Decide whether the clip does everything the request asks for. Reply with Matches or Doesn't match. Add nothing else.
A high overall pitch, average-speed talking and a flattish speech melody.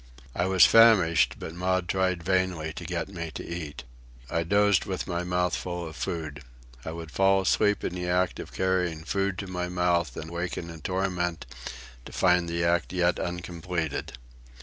Doesn't match